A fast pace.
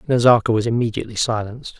No: slow, 135 wpm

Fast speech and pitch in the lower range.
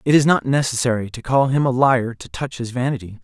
Yes: fast, 240 wpm; low, 130 Hz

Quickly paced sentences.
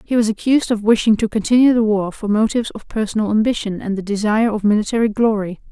Yes: fast, 210 wpm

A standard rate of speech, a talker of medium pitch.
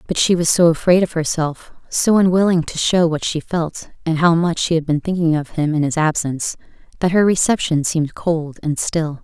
No: fast, 215 wpm; medium, 165 Hz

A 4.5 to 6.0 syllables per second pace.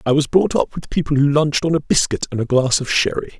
No: 6.3 syllables/s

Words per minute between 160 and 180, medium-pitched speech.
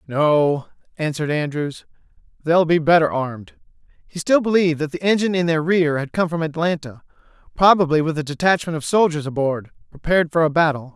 Yes: average, 165 wpm; medium, 160 Hz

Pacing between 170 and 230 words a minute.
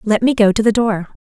No: fast, 295 wpm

